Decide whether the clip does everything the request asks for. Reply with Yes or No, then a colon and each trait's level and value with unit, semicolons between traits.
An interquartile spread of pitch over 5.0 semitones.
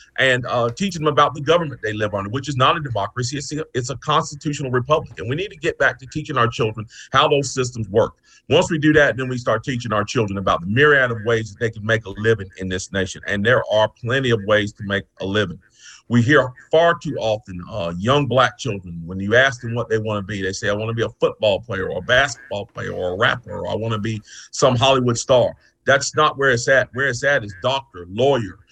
No: average, 4.7 semitones